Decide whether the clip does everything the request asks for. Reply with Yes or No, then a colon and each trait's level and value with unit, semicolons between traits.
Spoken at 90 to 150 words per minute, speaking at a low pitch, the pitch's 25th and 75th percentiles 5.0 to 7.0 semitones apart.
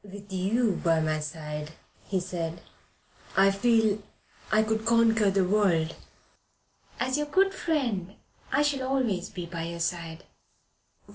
No: slow, 135 wpm; high, 195 Hz; wide, 5.4 semitones